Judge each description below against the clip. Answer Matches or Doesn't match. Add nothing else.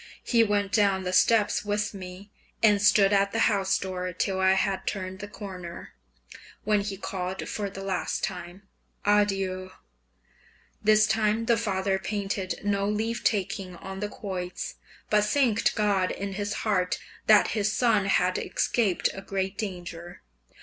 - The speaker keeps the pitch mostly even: Matches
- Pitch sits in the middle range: Doesn't match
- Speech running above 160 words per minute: Doesn't match